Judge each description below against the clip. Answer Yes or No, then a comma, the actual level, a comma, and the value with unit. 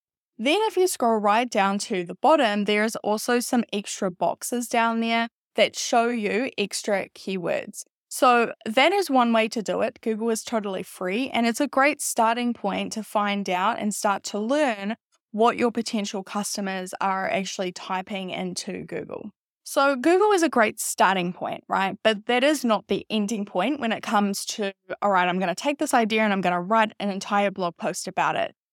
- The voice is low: No, high, 215 Hz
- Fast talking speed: No, average, 195 wpm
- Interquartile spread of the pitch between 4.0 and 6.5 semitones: No, average, 3.3 semitones